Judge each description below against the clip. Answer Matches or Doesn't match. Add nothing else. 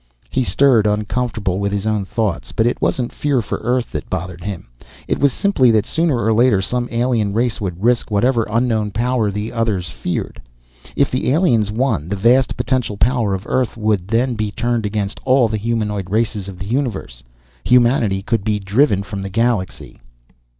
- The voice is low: Matches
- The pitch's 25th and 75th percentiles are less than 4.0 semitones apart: Matches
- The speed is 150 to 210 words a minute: Matches